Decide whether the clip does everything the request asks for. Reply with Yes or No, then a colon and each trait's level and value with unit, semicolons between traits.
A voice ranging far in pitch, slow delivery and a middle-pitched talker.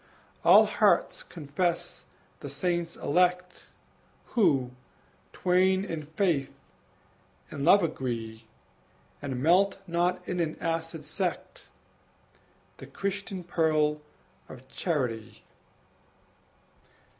No: average, 3.9 semitones; slow, 85 wpm; medium, 165 Hz